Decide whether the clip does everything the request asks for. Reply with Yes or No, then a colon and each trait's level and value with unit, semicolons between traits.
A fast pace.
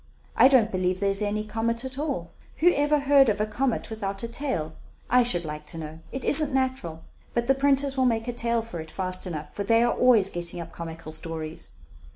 Yes: fast, 220 wpm